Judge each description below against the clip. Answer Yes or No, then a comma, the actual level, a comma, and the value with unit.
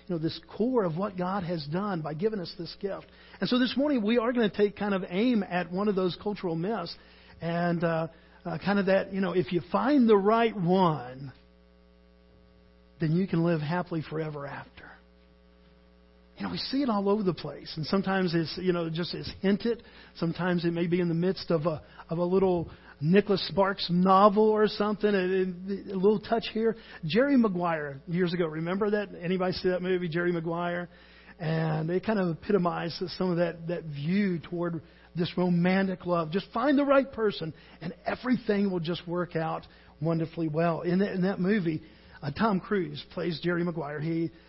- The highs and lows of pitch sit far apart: No, average, 3.4 semitones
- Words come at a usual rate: Yes, average, 195 wpm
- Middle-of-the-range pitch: Yes, medium, 180 Hz